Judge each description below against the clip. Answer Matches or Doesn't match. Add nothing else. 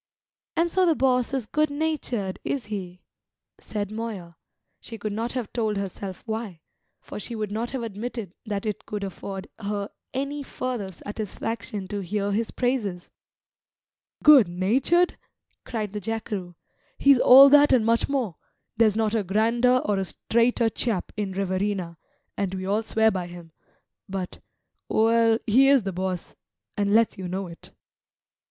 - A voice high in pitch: Matches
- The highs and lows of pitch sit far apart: Doesn't match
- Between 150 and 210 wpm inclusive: Matches